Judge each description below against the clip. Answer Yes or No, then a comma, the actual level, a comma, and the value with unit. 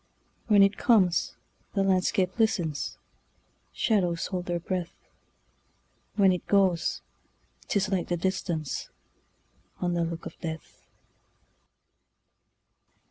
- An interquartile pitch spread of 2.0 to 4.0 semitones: Yes, narrow, 2.5 semitones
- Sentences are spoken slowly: Yes, slow, 90 wpm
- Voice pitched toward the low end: No, medium, 185 Hz